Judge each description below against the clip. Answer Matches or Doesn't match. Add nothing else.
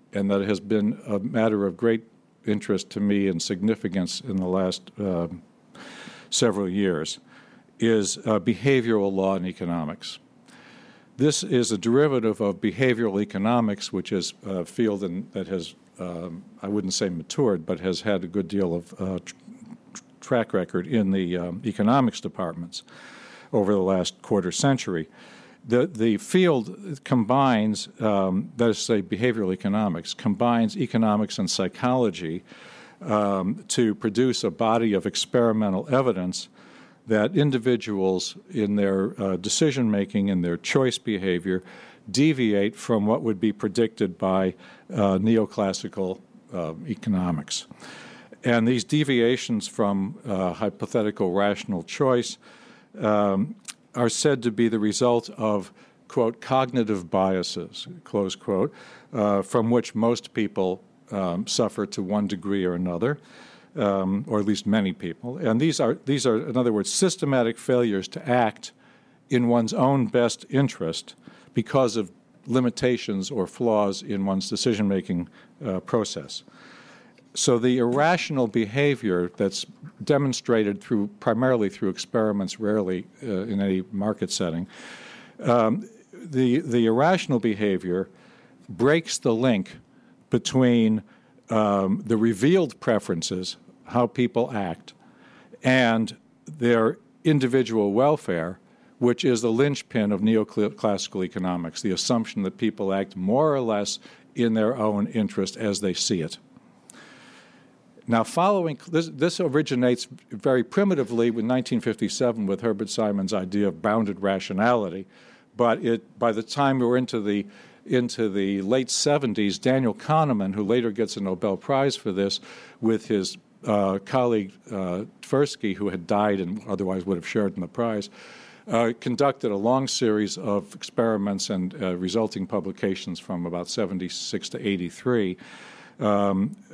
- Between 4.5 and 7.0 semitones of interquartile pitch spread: Doesn't match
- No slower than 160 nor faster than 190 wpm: Doesn't match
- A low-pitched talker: Matches